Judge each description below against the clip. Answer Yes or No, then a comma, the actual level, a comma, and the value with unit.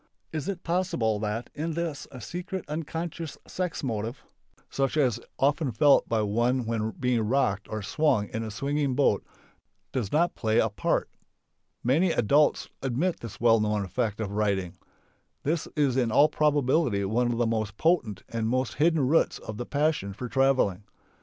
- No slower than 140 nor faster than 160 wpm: No, average, 170 wpm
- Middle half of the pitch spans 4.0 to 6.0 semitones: Yes, wide, 5.6 semitones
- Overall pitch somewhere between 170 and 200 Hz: No, low, 125 Hz